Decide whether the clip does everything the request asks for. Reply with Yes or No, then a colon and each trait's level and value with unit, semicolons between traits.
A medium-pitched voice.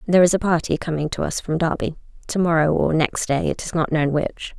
Yes: medium, 160 Hz